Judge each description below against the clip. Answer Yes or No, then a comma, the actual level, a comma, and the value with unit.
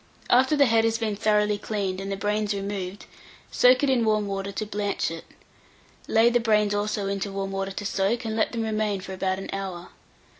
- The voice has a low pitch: No, high, 205 Hz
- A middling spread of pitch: No, narrow, 2.1 semitones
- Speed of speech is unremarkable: No, fast, 210 wpm